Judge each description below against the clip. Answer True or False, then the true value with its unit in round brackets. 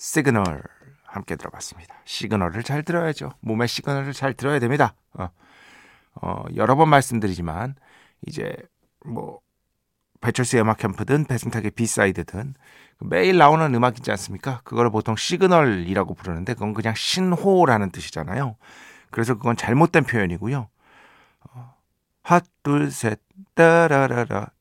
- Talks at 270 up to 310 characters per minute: True (305 characters per minute)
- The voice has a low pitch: True (120 Hz)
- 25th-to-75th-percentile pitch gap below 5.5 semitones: True (5.1 semitones)